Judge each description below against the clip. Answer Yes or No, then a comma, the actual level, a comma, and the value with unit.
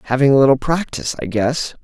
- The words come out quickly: No, average, 195 wpm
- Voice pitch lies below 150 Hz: Yes, medium, 140 Hz